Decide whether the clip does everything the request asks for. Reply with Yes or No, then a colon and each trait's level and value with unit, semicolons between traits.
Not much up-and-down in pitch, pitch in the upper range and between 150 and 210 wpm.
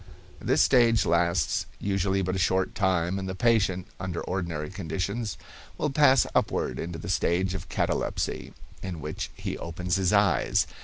No: narrow, 2.3 semitones; very low, 95 Hz; average, 155 wpm